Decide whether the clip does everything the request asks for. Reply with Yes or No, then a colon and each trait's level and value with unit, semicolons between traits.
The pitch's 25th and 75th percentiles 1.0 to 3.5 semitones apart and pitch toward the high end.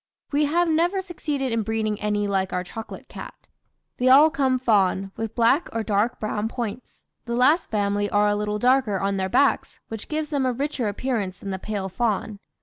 No: average, 4.6 semitones; high, 225 Hz